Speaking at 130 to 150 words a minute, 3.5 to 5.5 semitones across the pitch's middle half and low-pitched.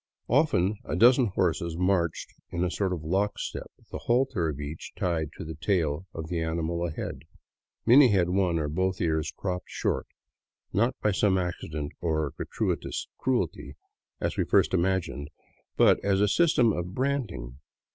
No: average, 160 wpm; average, 4.0 semitones; very low, 90 Hz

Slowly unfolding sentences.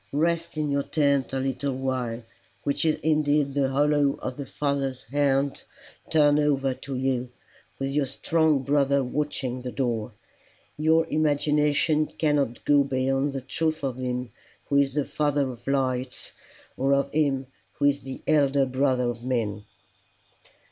No: average, 150 wpm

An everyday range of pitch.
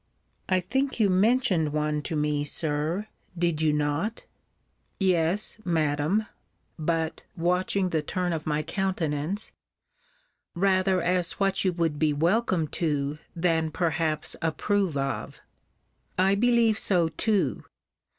Yes: average, 3.9 semitones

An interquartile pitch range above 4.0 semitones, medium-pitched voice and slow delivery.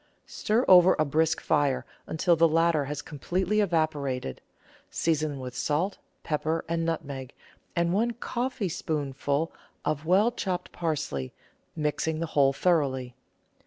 No: average, 3.6 semitones; medium, 160 Hz; slow, 125 wpm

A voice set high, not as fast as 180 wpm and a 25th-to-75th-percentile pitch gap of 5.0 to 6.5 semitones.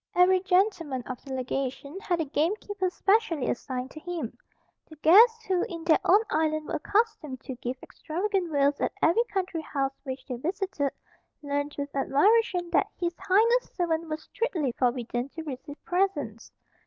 Yes: very high, 320 Hz; average, 160 wpm; average, 5.3 semitones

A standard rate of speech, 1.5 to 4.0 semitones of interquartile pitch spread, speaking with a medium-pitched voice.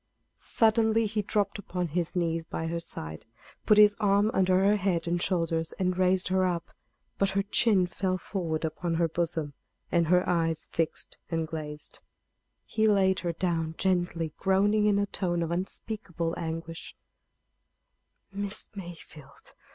Yes: average, 150 wpm; average, 3.1 semitones; medium, 180 Hz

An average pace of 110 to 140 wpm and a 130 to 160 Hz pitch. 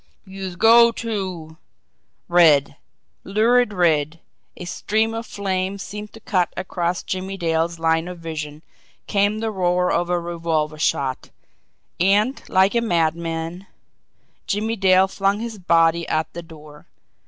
No: slow, 135 wpm; medium, 180 Hz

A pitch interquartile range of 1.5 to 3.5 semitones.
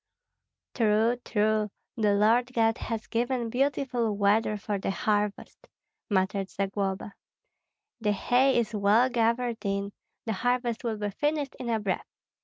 Yes: average, 2.8 semitones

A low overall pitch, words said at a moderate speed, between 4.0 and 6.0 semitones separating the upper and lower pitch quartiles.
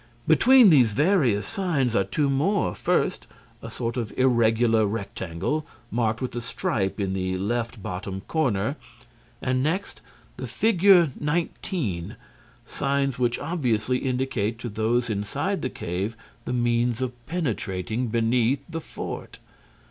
No: low, 120 Hz; slow, 130 wpm; average, 4.8 semitones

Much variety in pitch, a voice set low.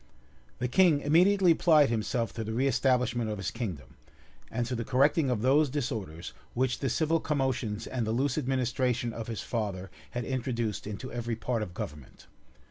No: average, 3.4 semitones; low, 120 Hz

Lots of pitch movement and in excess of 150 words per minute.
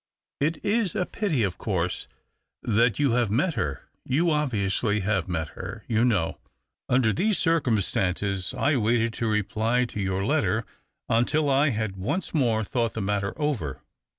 Yes: wide, 6.1 semitones; average, 160 wpm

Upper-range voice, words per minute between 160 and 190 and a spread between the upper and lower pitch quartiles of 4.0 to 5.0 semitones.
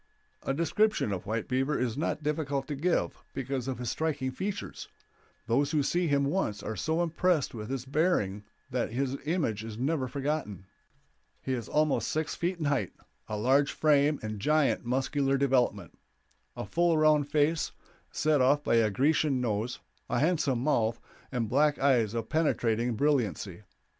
No: low, 135 Hz; average, 165 wpm; average, 4.6 semitones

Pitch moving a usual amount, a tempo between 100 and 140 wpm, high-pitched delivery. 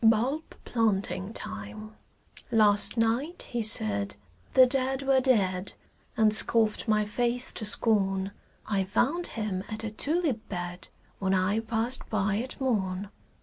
Yes: average, 3.9 semitones; slow, 135 wpm; high, 215 Hz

